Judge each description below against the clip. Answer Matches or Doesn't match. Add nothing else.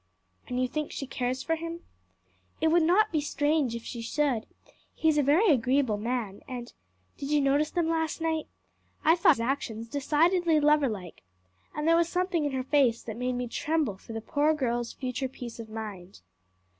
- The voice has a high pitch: Matches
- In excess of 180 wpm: Matches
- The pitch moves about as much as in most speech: Matches